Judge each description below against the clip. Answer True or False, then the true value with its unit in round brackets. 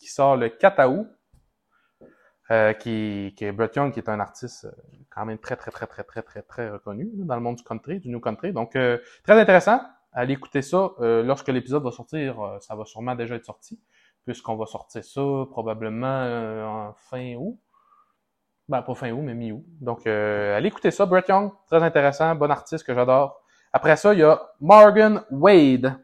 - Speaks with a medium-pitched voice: False (125 Hz)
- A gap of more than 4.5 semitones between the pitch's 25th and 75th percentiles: True (5.5 semitones)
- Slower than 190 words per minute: False (200 wpm)